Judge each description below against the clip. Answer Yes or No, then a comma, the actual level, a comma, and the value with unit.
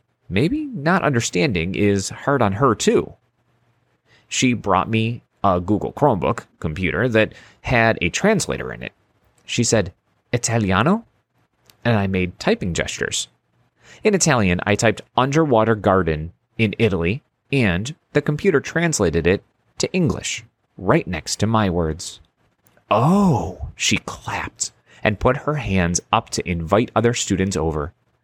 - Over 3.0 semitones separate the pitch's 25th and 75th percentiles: Yes, average, 4.7 semitones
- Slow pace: Yes, slow, 130 wpm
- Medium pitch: No, low, 110 Hz